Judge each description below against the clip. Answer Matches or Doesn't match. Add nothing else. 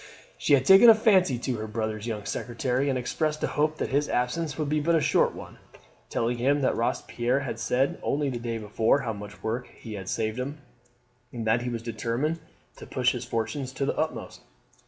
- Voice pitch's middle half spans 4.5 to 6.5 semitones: Doesn't match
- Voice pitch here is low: Matches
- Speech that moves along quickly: Matches